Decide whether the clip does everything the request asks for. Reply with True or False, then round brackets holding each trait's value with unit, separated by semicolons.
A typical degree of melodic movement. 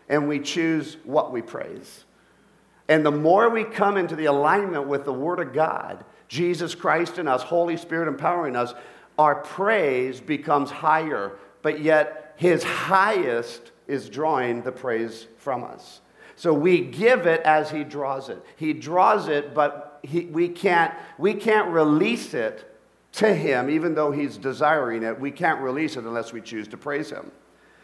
True (3.5 semitones)